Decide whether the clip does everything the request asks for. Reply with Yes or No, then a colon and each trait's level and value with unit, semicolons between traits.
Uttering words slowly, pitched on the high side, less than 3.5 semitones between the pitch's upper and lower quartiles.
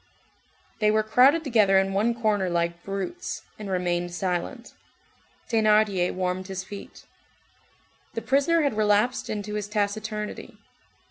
Yes: slow, 125 wpm; high, 210 Hz; average, 2.8 semitones